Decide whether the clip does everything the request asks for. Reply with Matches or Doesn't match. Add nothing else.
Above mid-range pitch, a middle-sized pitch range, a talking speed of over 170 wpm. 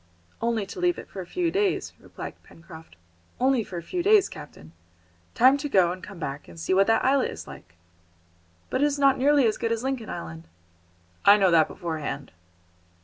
Doesn't match